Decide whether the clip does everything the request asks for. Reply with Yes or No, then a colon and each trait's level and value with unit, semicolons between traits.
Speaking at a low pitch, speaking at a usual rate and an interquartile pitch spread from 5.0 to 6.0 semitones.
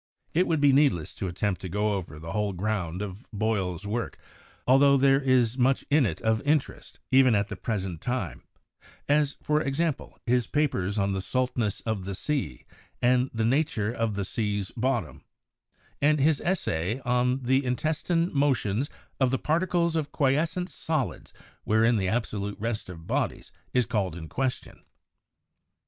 Yes: low, 120 Hz; average, 160 wpm; wide, 5.4 semitones